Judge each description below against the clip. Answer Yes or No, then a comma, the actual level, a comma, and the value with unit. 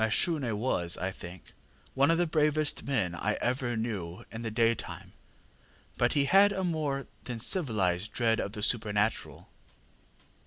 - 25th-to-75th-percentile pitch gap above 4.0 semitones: Yes, wide, 5.5 semitones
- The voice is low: Yes, low, 115 Hz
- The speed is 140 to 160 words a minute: Yes, average, 150 wpm